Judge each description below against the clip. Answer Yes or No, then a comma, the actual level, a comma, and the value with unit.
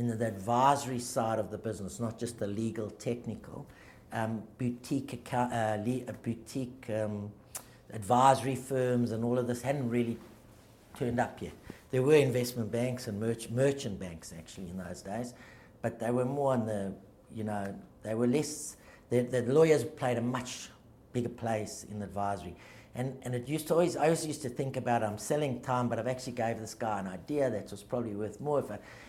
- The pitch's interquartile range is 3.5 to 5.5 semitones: No, average, 2.9 semitones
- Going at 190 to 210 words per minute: Yes, average, 195 wpm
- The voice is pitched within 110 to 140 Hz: Yes, low, 120 Hz